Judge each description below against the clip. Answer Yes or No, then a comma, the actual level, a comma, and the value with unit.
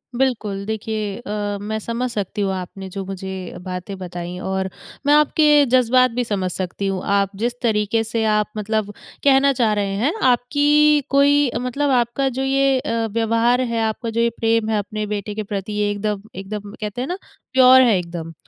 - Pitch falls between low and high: No, high, 220 Hz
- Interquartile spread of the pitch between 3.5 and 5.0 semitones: Yes, average, 4.1 semitones